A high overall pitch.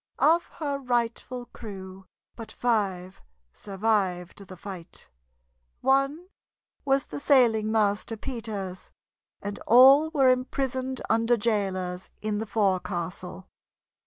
Yes: high, 220 Hz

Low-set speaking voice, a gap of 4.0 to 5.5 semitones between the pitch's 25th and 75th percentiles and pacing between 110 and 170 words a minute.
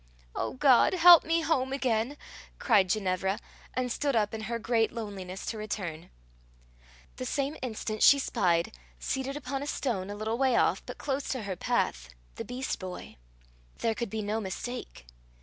No: high, 225 Hz; average, 4.9 semitones; average, 165 wpm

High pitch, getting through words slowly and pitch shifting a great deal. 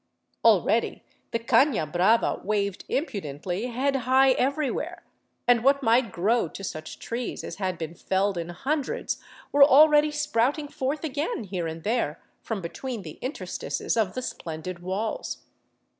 No: high, 230 Hz; average, 145 wpm; wide, 6.6 semitones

